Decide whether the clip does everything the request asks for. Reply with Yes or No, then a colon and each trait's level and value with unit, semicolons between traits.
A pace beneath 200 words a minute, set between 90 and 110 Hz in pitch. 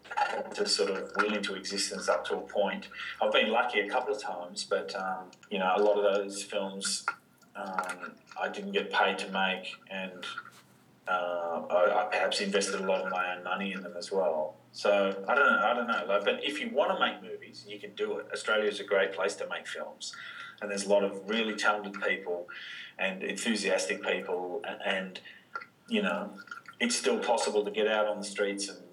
No: fast, 205 wpm; low, 100 Hz